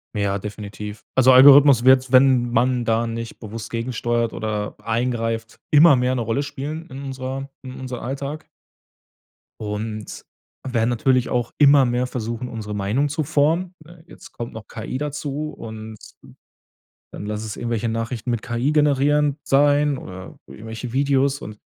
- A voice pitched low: Yes, low, 125 Hz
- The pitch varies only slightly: No, average, 3.6 semitones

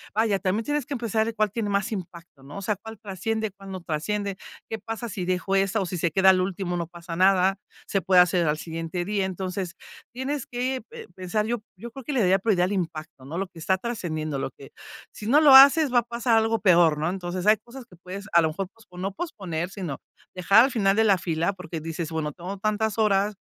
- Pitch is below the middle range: No, high, 195 Hz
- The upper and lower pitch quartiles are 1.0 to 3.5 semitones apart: No, average, 4.0 semitones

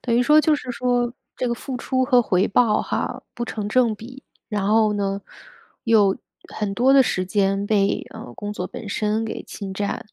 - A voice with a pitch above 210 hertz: Yes, high, 220 Hz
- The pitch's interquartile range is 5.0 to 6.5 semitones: No, average, 3.5 semitones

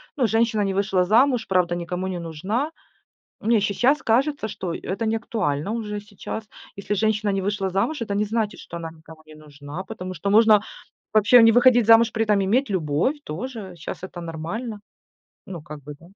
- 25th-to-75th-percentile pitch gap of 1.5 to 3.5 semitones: No, average, 4.3 semitones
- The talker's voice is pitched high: Yes, high, 205 Hz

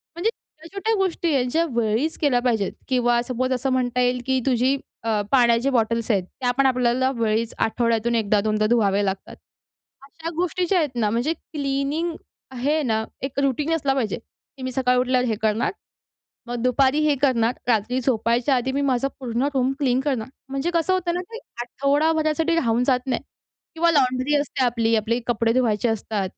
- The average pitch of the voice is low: No, very high, 255 Hz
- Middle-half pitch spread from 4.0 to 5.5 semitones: No, average, 3.3 semitones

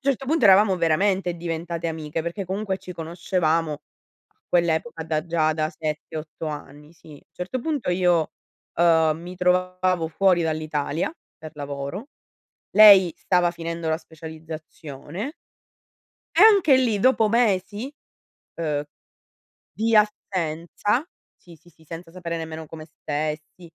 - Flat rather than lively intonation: No, average, 3.3 semitones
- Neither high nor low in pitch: Yes, medium, 170 Hz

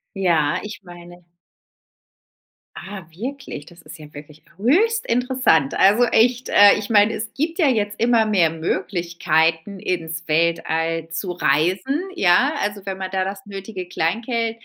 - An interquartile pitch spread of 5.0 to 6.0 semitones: Yes, wide, 5.4 semitones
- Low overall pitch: No, high, 190 Hz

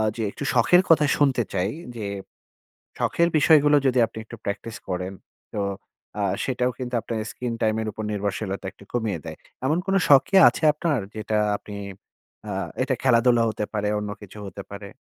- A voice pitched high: No, low, 115 Hz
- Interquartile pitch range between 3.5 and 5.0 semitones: Yes, average, 4.3 semitones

